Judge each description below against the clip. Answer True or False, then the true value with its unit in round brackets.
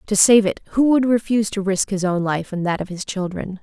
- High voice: True (200 Hz)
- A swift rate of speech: True (265 wpm)